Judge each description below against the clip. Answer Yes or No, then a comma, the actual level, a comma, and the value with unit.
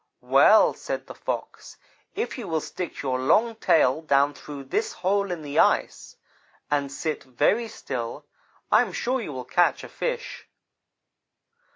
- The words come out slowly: No, average, 155 wpm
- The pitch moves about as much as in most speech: No, wide, 7.3 semitones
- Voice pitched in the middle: Yes, medium, 160 Hz